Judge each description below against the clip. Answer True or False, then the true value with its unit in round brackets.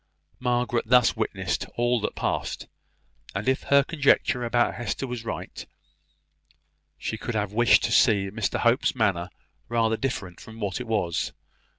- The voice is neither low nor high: False (115 Hz)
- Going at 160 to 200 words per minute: False (150 wpm)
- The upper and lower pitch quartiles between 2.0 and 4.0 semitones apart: True (2.9 semitones)